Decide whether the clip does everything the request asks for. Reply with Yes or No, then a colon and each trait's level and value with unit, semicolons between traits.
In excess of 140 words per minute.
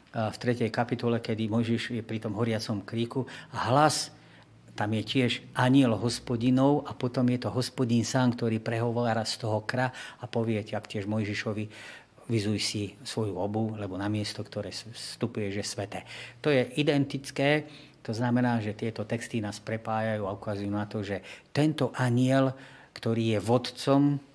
Yes: average, 160 wpm